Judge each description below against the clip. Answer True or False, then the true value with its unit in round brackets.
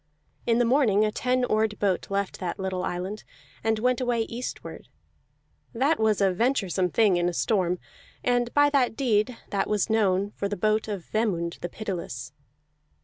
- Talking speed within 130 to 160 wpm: False (170 wpm)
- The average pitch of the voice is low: False (215 Hz)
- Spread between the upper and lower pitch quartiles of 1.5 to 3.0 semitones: False (3.9 semitones)